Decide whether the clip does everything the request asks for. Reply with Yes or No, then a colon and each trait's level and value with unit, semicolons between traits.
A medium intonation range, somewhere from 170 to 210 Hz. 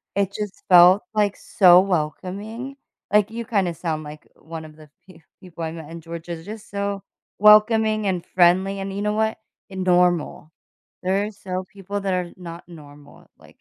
Yes: average, 3.2 semitones; medium, 185 Hz